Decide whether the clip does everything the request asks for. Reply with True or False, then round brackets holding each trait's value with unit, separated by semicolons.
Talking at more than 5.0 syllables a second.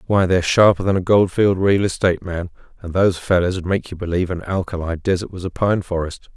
True (6.1 syllables/s)